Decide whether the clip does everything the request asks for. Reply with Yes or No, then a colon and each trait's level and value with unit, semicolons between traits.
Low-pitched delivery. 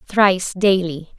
No: medium, 185 Hz